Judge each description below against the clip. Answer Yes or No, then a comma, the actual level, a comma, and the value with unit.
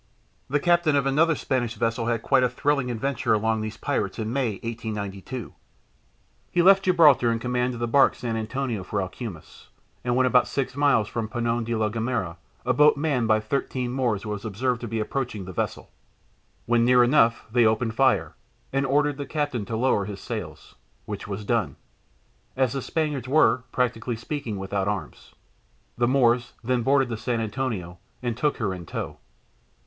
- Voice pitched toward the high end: No, low, 120 Hz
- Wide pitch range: No, average, 3.5 semitones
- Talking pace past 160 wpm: Yes, average, 180 wpm